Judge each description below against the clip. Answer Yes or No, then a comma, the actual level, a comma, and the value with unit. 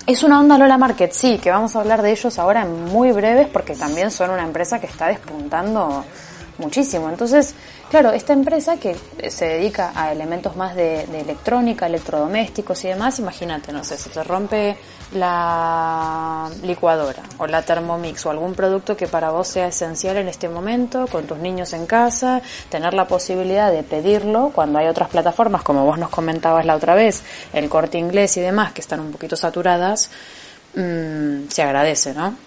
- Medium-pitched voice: Yes, medium, 180 Hz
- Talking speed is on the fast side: No, average, 180 wpm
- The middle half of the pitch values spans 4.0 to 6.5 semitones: Yes, average, 4.8 semitones